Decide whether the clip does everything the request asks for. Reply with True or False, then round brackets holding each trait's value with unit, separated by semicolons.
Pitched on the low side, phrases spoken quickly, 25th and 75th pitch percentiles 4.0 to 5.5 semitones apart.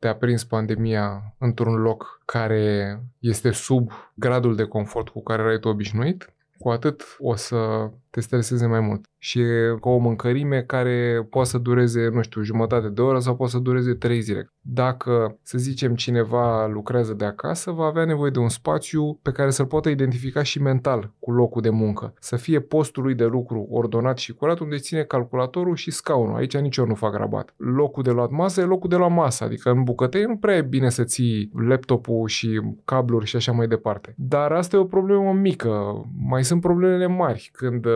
False (120 Hz; 195 wpm; 3.3 semitones)